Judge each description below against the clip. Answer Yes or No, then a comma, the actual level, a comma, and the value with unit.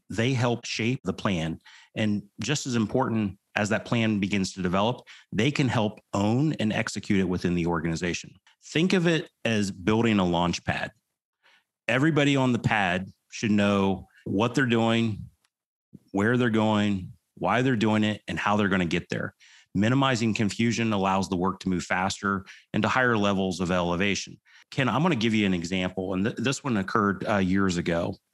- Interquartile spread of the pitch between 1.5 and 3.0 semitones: No, average, 3.7 semitones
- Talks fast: No, average, 180 wpm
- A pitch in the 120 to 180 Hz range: No, low, 105 Hz